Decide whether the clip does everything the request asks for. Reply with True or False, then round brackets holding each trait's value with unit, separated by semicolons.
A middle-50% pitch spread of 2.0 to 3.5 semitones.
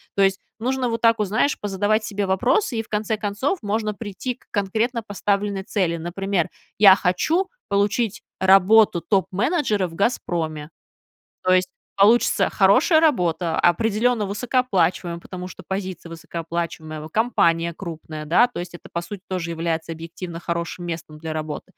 False (4.4 semitones)